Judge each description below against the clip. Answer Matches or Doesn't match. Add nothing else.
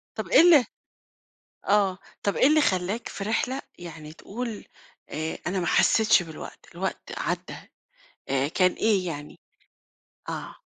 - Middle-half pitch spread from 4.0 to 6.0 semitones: Matches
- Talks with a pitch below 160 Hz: Doesn't match